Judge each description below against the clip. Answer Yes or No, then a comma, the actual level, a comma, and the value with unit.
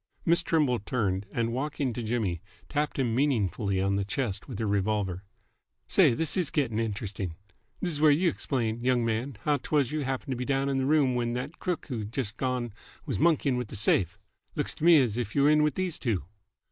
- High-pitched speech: No, low, 125 Hz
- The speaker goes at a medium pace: No, fast, 215 wpm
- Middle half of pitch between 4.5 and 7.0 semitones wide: Yes, average, 5.2 semitones